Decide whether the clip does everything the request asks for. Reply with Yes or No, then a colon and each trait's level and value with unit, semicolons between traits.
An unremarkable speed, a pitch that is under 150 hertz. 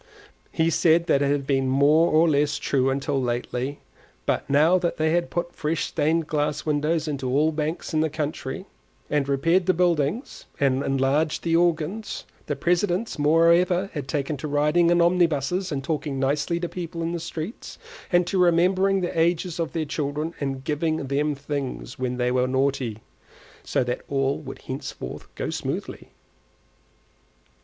No: average, 165 wpm; medium, 155 Hz